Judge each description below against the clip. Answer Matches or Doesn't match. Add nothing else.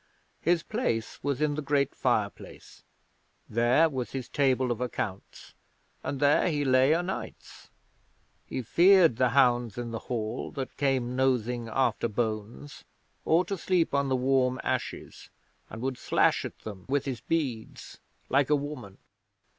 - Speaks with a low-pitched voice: Matches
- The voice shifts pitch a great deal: Doesn't match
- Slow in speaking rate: Doesn't match